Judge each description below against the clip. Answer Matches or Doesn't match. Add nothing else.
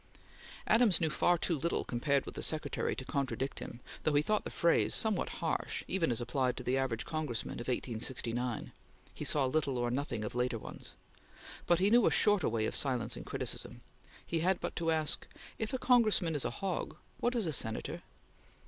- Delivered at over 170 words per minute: Matches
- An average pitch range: Doesn't match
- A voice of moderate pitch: Matches